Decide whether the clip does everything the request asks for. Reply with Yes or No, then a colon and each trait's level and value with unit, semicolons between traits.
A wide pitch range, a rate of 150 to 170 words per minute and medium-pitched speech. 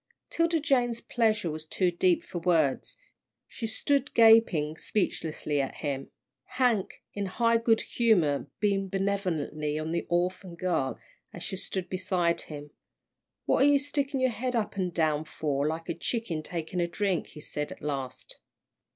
Yes: wide, 6.5 semitones; average, 160 wpm; medium, 180 Hz